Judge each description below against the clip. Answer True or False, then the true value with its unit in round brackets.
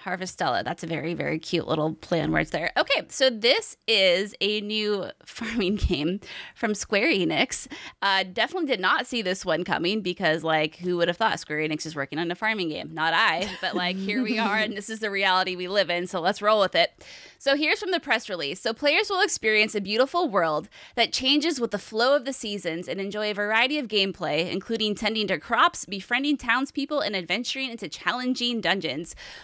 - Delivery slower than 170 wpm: False (205 wpm)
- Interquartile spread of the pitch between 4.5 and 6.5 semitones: True (5.1 semitones)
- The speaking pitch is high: True (210 Hz)